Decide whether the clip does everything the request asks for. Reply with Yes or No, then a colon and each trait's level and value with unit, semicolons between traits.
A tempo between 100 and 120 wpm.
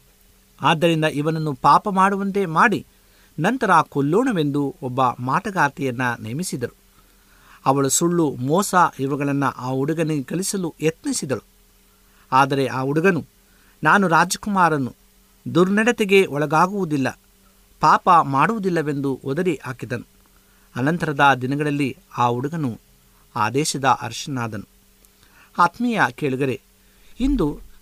No: average, 85 wpm